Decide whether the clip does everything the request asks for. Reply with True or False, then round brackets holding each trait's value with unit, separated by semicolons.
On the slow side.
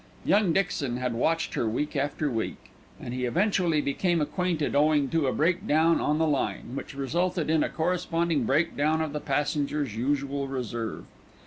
False (160 wpm)